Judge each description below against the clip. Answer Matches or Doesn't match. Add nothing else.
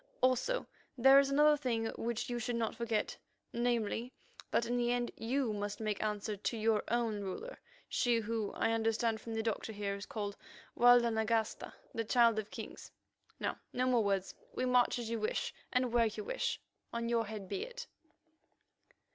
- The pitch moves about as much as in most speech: Doesn't match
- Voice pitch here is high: Matches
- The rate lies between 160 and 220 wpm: Matches